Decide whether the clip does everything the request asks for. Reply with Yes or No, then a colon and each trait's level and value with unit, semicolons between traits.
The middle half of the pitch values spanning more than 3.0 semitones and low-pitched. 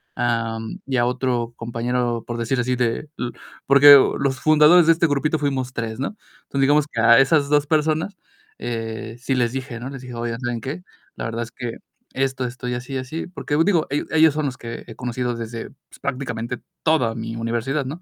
Yes: average, 3.5 semitones; low, 125 Hz